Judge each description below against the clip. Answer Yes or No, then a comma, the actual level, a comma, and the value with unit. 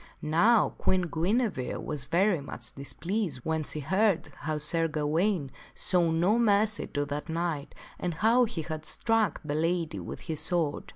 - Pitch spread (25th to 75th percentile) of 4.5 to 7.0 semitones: Yes, average, 4.9 semitones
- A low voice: No, medium, 165 Hz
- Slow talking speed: No, average, 165 wpm